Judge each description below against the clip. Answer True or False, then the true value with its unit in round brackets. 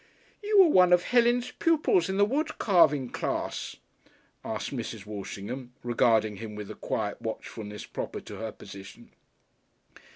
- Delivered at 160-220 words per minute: False (140 wpm)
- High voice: False (130 Hz)